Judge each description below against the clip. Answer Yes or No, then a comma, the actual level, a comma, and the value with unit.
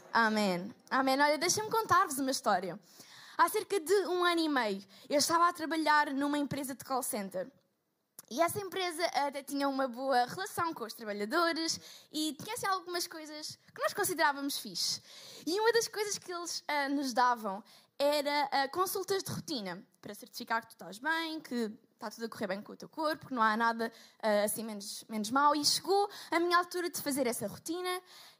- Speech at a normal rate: No, fast, 190 wpm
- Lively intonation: Yes, wide, 7.0 semitones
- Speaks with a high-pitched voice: Yes, very high, 285 Hz